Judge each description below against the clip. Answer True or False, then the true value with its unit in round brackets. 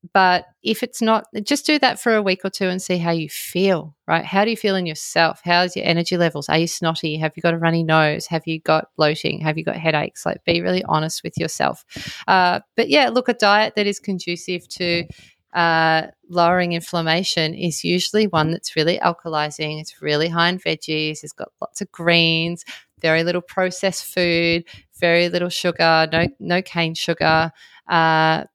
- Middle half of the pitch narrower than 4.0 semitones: True (2.6 semitones)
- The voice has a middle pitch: True (170 Hz)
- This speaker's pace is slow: False (195 wpm)